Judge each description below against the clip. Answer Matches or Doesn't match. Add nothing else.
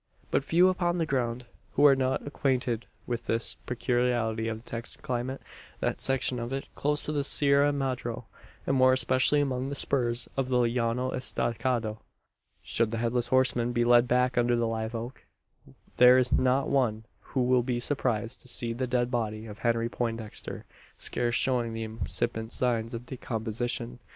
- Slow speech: Doesn't match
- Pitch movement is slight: Matches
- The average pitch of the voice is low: Matches